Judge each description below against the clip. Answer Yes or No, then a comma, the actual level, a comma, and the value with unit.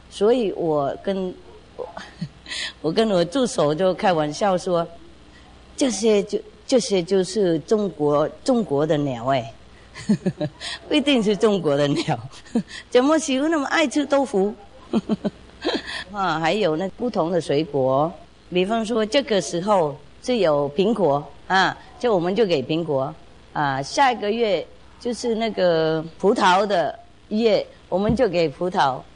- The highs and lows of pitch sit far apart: Yes, wide, 7.2 semitones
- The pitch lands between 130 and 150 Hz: No, high, 190 Hz